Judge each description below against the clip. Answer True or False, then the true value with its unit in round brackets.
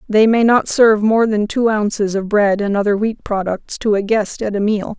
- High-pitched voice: True (210 Hz)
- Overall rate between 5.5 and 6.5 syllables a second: False (5.0 syllables/s)